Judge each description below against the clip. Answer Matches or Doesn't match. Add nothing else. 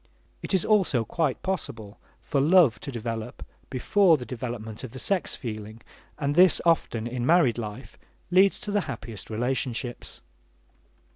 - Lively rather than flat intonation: Matches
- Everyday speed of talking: Matches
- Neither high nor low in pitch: Doesn't match